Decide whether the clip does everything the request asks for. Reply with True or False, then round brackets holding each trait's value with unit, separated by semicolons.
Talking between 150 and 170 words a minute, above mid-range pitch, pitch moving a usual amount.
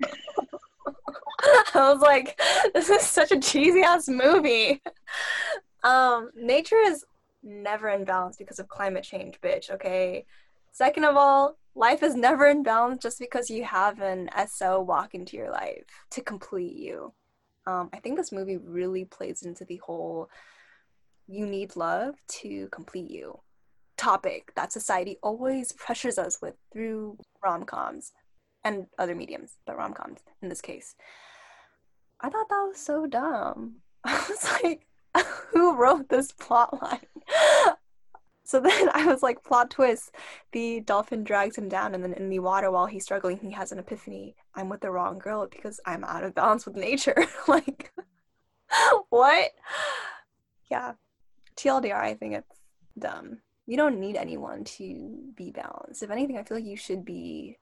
False (155 wpm; 235 Hz; 7.0 semitones)